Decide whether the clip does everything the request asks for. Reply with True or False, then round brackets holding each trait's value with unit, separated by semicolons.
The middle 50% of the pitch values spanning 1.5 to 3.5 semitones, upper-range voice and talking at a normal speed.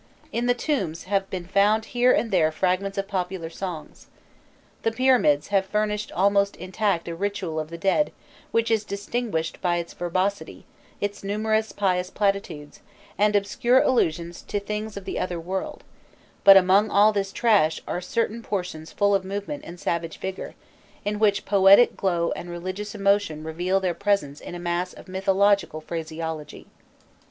True (3.0 semitones; 195 Hz; 160 wpm)